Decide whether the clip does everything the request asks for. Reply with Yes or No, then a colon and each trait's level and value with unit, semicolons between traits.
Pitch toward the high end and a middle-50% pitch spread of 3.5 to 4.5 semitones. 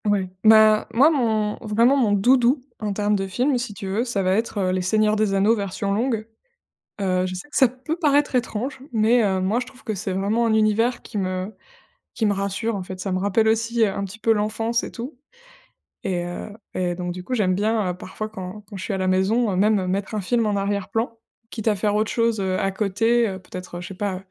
No: high, 210 Hz; average, 3.1 semitones